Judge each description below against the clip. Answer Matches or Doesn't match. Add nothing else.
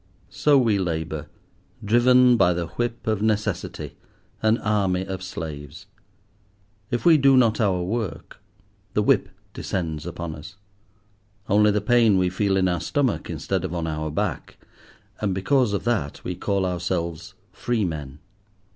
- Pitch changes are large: Doesn't match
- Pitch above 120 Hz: Doesn't match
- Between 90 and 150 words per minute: Matches